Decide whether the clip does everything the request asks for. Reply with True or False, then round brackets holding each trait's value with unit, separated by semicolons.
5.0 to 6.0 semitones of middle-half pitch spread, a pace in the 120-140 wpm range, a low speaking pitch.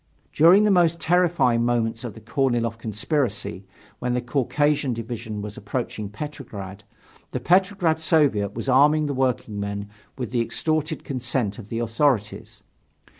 True (5.4 semitones; 135 wpm; 125 Hz)